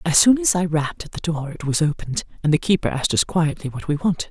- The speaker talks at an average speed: No, fast, 280 wpm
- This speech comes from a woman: Yes, female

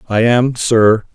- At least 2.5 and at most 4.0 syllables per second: Yes, 3.5 syllables/s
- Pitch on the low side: Yes, low, 115 Hz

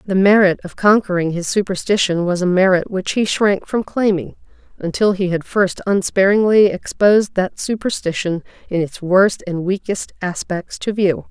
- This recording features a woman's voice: Yes, female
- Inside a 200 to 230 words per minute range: No, average, 160 wpm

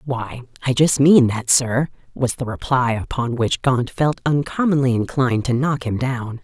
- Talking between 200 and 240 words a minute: No, average, 175 wpm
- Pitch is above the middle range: No, low, 130 Hz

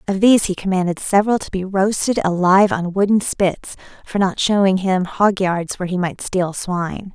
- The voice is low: No, high, 190 Hz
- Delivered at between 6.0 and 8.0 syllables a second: No, 5.2 syllables/s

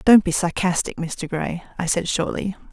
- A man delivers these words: No, female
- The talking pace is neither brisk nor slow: Yes, average, 175 wpm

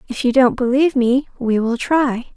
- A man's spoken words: No, female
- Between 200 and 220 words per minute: Yes, fast, 205 wpm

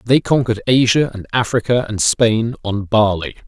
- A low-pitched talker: Yes, low, 115 Hz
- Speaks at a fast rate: No, average, 155 wpm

